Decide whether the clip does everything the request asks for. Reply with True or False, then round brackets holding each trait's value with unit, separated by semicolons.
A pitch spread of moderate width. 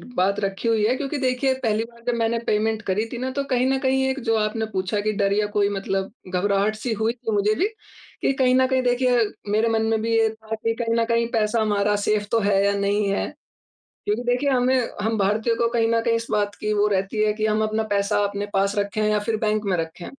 False (2.3 semitones)